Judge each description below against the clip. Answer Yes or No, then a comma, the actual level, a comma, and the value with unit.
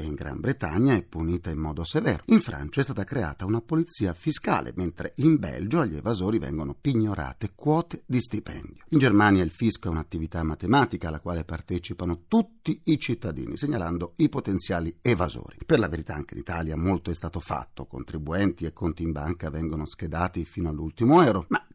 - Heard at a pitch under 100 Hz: Yes, very low, 90 Hz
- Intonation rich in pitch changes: Yes, wide, 6.9 semitones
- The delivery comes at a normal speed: No, fast, 175 wpm